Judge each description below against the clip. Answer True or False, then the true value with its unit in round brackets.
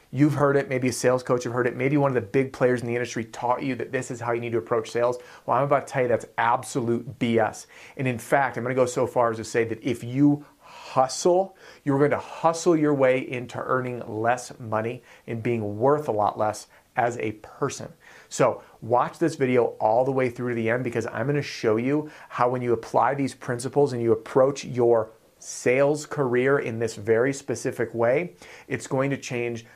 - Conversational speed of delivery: False (220 wpm)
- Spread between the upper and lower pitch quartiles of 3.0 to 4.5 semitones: False (2.6 semitones)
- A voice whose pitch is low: True (125 Hz)